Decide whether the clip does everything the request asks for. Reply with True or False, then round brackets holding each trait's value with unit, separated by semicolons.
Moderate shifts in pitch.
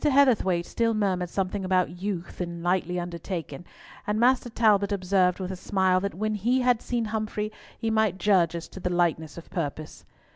True (3.5 semitones)